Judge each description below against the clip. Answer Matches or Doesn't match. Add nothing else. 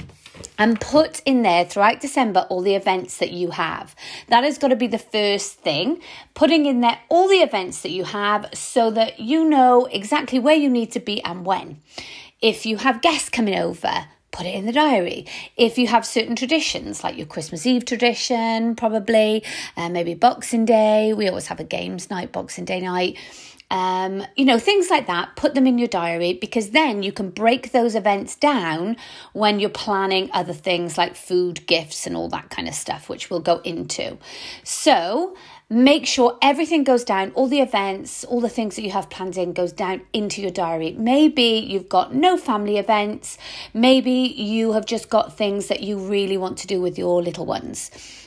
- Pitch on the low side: Doesn't match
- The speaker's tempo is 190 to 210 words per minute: Matches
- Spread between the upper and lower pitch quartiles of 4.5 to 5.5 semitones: Matches